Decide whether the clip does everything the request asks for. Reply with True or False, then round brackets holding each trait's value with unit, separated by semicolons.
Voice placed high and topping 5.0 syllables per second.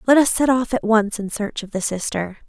True (225 Hz; 5.4 syllables/s)